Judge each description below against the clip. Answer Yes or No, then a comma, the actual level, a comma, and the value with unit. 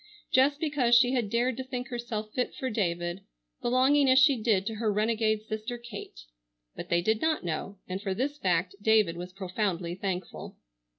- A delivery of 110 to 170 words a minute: No, average, 180 wpm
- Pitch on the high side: Yes, high, 220 Hz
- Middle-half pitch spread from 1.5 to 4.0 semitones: No, average, 4.9 semitones